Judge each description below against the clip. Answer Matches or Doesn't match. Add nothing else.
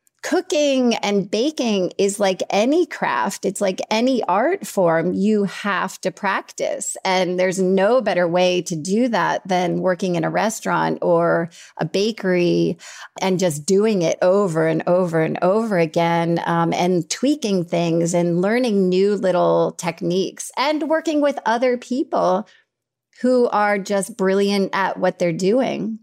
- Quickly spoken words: Doesn't match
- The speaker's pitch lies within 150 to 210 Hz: Matches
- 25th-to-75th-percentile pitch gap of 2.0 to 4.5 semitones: Matches